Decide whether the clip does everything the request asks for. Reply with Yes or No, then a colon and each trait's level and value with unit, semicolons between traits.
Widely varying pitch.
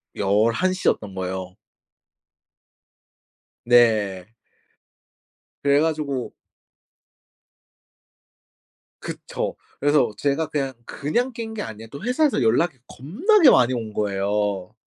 Yes: wide, 7.6 semitones